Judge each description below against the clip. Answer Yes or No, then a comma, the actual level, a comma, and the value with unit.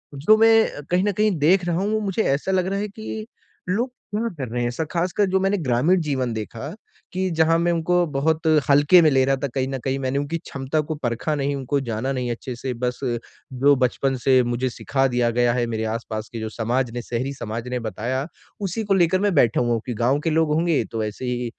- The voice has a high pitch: No, medium, 140 Hz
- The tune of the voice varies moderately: No, wide, 6.0 semitones